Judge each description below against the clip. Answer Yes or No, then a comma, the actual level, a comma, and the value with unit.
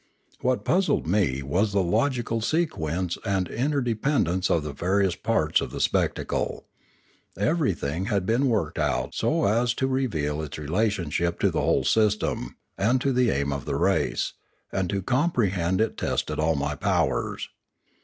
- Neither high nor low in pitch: No, very low, 95 Hz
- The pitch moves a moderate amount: No, wide, 6.9 semitones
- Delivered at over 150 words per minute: Yes, average, 160 wpm